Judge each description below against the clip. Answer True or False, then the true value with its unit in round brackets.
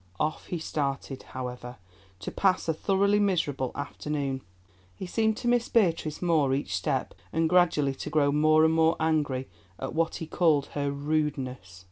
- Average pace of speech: True (160 wpm)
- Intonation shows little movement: False (3.3 semitones)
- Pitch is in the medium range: True (155 Hz)